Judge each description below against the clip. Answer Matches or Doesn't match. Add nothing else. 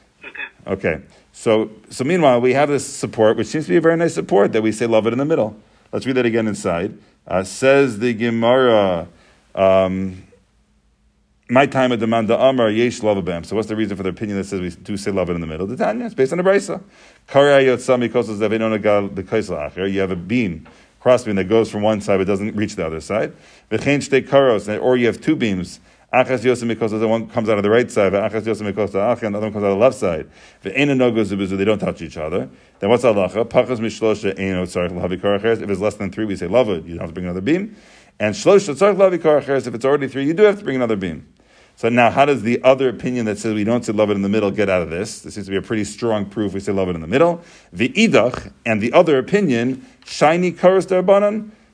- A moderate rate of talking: Doesn't match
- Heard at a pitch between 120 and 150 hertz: Doesn't match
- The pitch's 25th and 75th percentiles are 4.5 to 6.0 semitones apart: Matches